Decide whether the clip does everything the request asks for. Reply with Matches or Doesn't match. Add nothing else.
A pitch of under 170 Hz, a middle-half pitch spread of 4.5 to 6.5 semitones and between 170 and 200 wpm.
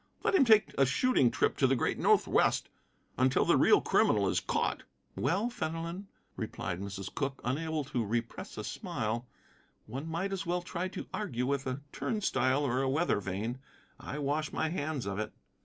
Matches